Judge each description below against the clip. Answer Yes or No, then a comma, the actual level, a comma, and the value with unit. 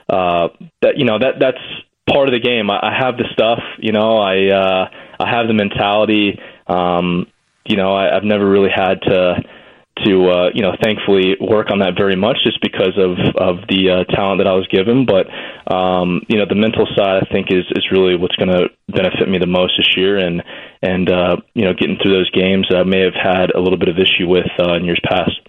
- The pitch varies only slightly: Yes, narrow, 1.6 semitones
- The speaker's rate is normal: No, fast, 230 wpm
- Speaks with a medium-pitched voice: No, very low, 95 Hz